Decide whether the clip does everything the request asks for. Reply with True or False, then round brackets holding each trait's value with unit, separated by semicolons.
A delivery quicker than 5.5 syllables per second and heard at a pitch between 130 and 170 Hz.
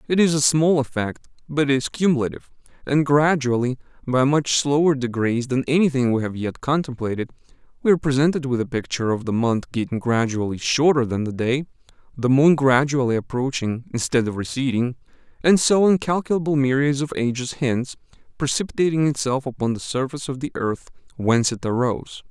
True (5.8 syllables/s; 135 Hz)